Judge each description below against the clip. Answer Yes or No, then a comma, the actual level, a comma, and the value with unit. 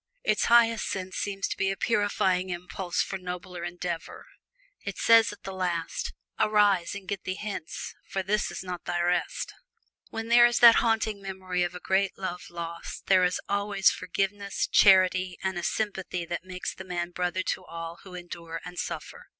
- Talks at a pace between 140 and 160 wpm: No, average, 180 wpm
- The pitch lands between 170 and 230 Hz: Yes, medium, 185 Hz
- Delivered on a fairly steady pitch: Yes, narrow, 2.2 semitones